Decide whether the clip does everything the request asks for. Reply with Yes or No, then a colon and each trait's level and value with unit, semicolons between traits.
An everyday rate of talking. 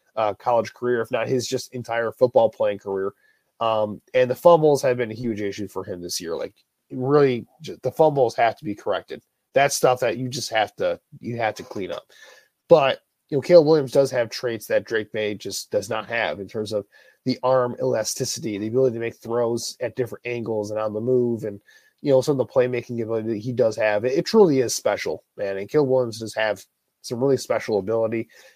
No: fast, 220 wpm